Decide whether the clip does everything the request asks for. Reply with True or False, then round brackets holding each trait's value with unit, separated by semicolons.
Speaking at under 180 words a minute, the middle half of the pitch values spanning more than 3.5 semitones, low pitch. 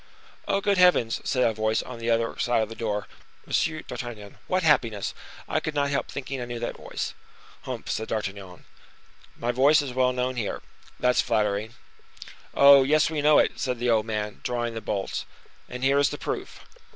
False (190 wpm; 4.0 semitones; 120 Hz)